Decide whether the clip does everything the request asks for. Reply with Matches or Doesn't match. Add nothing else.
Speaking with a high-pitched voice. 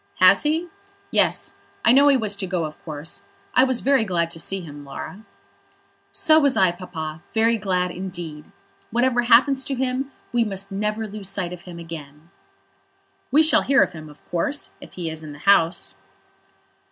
Matches